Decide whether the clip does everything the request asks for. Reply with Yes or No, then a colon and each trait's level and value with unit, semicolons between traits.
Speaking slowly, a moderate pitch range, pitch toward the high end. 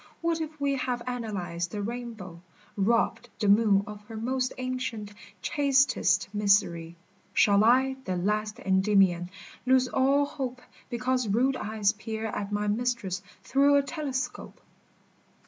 Yes: slow, 130 wpm; average, 4.2 semitones; high, 225 Hz